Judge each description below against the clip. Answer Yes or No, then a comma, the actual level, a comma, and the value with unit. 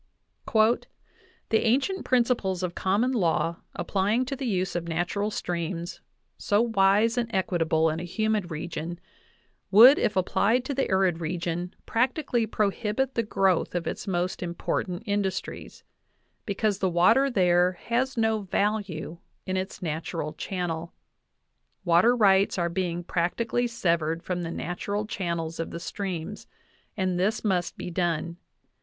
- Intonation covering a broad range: No, average, 4.0 semitones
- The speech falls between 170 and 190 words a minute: No, average, 140 wpm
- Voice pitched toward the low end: No, high, 190 Hz